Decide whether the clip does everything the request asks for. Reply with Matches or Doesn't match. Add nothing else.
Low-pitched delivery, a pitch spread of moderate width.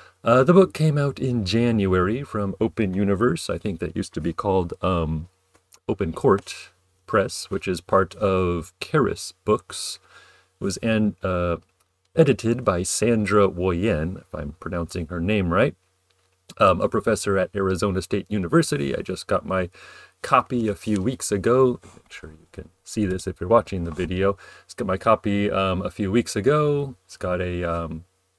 Matches